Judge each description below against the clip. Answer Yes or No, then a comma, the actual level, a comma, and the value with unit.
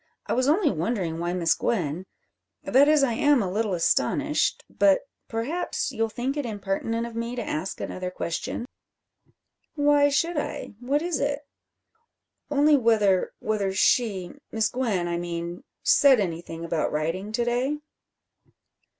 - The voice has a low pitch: No, high, 225 Hz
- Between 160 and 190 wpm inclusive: No, average, 145 wpm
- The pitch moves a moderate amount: No, wide, 7.1 semitones